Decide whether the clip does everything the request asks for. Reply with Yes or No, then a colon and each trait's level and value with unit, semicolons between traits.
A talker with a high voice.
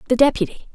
Yes: high, 235 Hz